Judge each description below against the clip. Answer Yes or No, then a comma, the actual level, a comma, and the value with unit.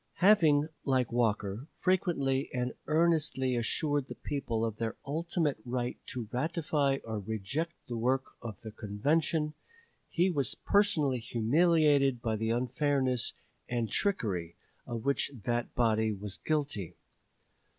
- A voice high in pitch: No, low, 130 Hz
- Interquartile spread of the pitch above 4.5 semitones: Yes, average, 5.0 semitones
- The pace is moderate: No, slow, 125 wpm